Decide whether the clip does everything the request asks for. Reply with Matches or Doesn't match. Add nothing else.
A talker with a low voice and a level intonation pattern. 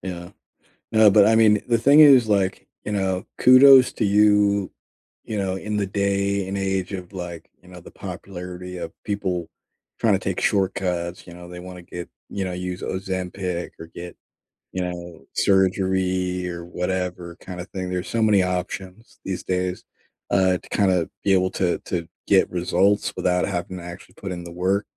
Matches